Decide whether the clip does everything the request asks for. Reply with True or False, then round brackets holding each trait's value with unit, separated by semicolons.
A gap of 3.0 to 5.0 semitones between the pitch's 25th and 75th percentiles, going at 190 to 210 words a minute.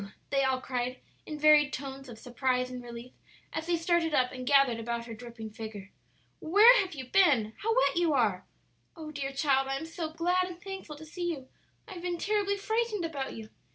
False (5.6 semitones; 205 wpm)